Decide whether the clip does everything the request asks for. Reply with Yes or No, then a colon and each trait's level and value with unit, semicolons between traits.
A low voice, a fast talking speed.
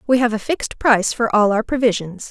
No: high, 225 Hz; fast, 235 wpm